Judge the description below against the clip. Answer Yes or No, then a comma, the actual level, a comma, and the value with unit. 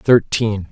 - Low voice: Yes, low, 105 Hz